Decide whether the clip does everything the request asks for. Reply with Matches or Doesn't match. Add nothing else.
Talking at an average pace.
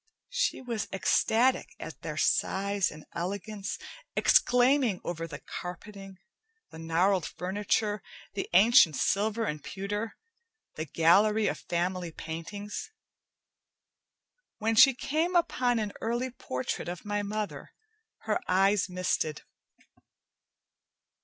Doesn't match